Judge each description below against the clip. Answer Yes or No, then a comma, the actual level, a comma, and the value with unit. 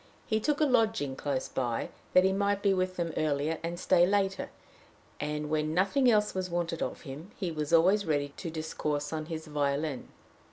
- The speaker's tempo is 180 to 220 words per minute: Yes, average, 190 wpm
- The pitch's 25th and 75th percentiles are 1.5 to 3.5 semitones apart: No, average, 4.3 semitones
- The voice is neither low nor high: Yes, medium, 165 Hz